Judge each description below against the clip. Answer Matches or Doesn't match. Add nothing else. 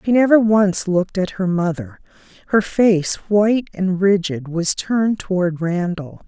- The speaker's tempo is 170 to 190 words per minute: Doesn't match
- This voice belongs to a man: Doesn't match